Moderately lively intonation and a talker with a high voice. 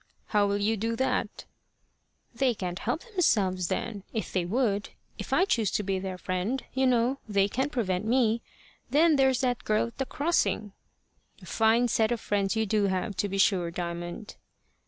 Yes: average, 4.1 semitones; high, 215 Hz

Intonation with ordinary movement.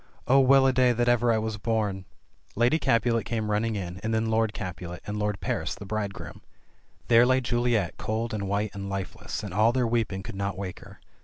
Yes: average, 3.0 semitones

